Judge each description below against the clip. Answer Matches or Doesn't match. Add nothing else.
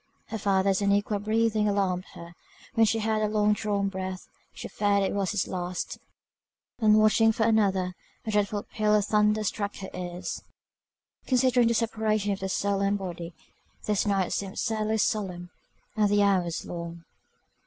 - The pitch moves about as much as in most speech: Doesn't match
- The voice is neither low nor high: Doesn't match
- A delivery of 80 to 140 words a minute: Doesn't match